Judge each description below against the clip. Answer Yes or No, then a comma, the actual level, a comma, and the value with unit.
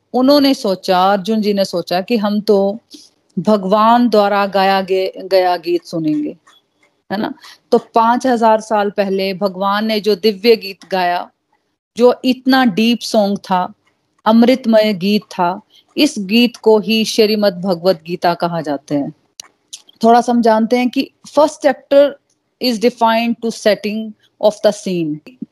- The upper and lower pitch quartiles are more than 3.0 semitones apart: Yes, average, 3.6 semitones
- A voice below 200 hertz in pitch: No, high, 215 Hz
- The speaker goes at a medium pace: Yes, average, 140 wpm